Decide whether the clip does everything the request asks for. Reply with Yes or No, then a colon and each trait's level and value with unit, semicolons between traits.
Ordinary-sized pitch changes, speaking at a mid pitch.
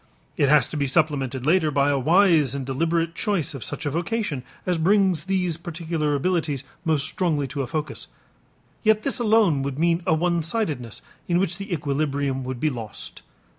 Yes: average, 4.1 semitones; medium, 155 Hz